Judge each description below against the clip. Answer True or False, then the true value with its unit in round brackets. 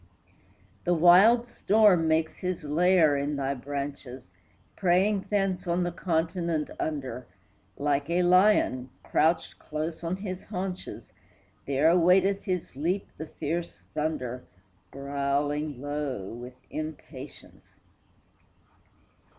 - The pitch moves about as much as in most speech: True (4.2 semitones)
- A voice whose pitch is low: False (160 Hz)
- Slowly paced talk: True (105 wpm)